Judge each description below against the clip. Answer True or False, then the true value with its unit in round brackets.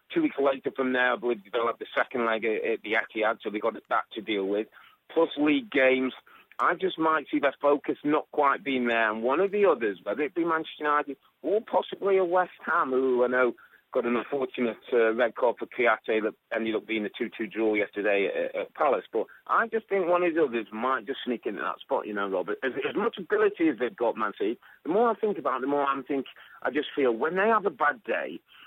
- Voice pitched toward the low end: False (145 Hz)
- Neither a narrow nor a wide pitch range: False (8.0 semitones)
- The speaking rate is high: True (245 wpm)